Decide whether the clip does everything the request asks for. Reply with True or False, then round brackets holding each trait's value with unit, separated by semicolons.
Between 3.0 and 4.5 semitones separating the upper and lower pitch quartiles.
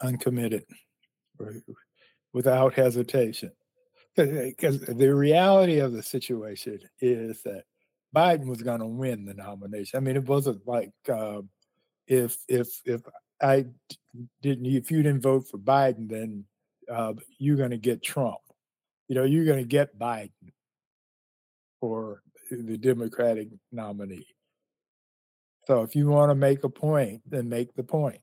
True (3.3 semitones)